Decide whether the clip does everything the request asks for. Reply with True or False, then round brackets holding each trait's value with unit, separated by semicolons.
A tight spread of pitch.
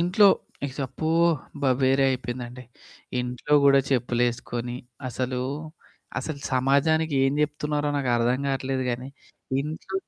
False (3.0 semitones)